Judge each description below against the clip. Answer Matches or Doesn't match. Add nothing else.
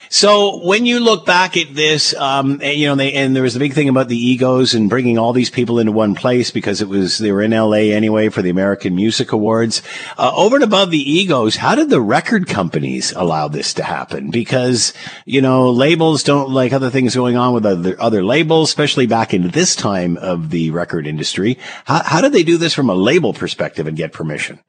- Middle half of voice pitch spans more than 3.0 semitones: Matches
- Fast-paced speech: Matches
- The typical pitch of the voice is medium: Doesn't match